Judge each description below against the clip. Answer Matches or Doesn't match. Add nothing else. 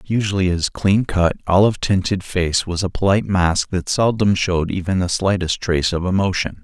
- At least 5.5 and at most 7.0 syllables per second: Doesn't match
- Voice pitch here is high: Doesn't match